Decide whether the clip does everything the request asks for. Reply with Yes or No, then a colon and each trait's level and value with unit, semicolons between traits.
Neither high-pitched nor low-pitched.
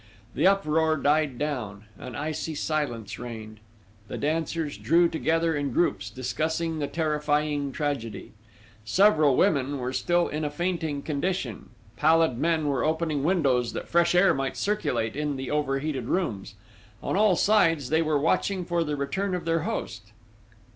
Yes: medium, 150 Hz